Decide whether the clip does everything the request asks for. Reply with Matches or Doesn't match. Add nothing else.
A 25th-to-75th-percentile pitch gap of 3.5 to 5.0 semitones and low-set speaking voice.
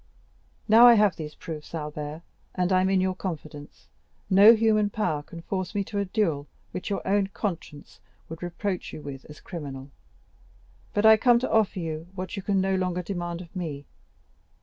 Doesn't match